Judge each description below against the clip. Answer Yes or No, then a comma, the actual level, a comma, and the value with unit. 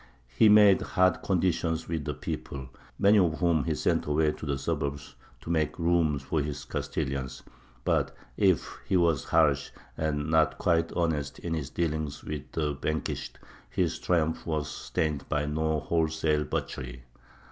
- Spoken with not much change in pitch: Yes, narrow, 2.2 semitones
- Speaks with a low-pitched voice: Yes, very low, 80 Hz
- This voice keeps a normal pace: Yes, average, 155 wpm